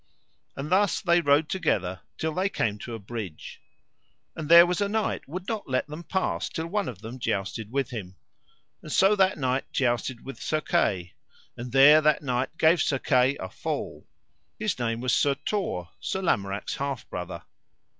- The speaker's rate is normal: Yes, average, 180 wpm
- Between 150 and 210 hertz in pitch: No, low, 135 Hz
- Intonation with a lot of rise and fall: Yes, wide, 6.8 semitones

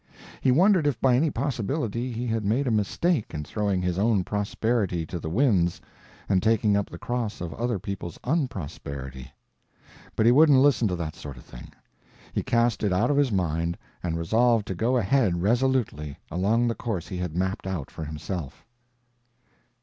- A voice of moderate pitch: No, low, 105 Hz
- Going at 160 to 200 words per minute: Yes, average, 180 wpm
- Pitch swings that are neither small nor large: No, wide, 5.8 semitones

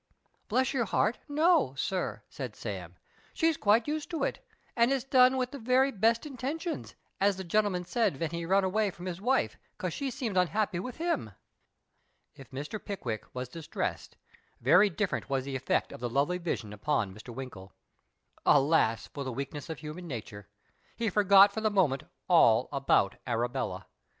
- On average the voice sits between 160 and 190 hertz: Yes, medium, 185 Hz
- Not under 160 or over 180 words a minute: Yes, average, 175 wpm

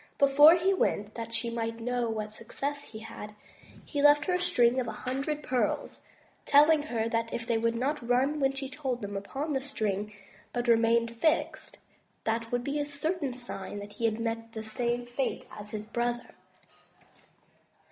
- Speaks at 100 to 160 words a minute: No, average, 180 wpm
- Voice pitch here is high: Yes, high, 240 Hz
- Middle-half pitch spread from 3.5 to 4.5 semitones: Yes, average, 3.8 semitones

